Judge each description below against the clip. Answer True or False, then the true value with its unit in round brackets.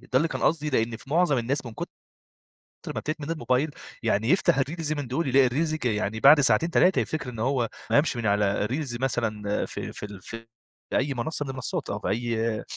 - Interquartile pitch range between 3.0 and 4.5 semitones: False (4.9 semitones)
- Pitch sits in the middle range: False (130 Hz)